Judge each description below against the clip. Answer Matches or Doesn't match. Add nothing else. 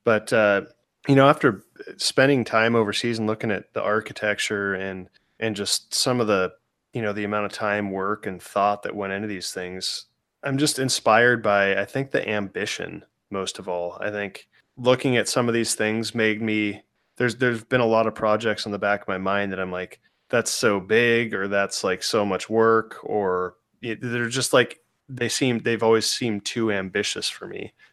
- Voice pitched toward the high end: Doesn't match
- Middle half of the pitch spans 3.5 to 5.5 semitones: Doesn't match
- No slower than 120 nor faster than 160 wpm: Doesn't match